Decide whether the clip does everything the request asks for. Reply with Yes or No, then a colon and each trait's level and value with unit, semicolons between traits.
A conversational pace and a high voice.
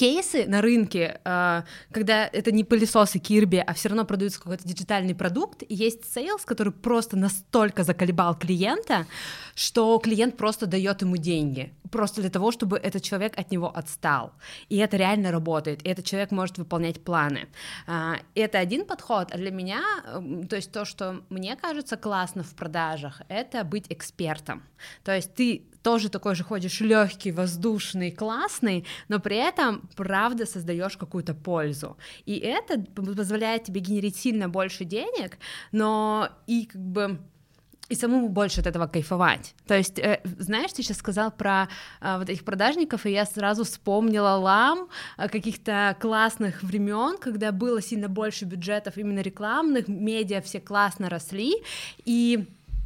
Yes: average, 150 wpm; high, 200 Hz